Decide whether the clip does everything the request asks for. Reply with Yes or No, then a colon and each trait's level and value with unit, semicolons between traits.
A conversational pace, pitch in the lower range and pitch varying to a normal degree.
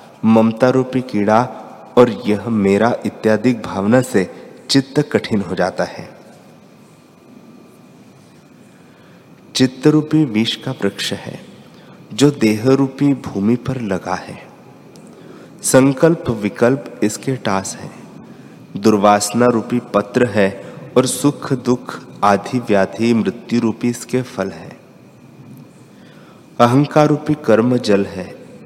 No: slow, 105 wpm; low, 120 Hz; average, 3.6 semitones